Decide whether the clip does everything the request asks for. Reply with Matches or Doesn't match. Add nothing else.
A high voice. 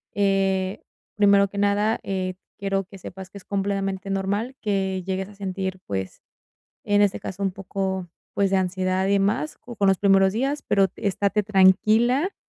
Matches